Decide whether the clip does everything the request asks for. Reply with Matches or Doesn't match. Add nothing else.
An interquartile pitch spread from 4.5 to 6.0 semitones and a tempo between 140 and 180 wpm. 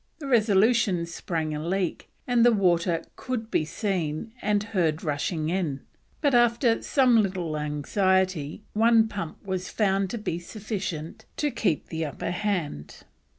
Matches